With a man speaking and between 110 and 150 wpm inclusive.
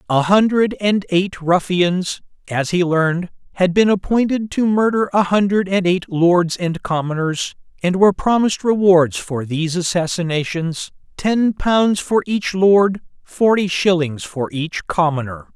Yes: male; average, 145 wpm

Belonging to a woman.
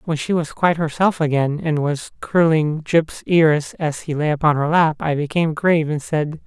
No: male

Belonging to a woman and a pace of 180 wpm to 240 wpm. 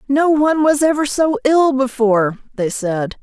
No: female; average, 165 wpm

